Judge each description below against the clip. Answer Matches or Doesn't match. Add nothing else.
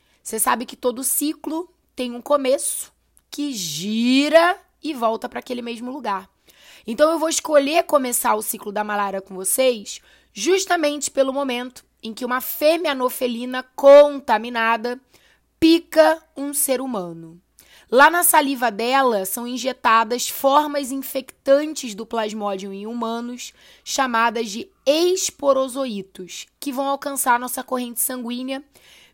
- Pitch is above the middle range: Matches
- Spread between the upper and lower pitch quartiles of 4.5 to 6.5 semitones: Doesn't match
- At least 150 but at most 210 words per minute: Doesn't match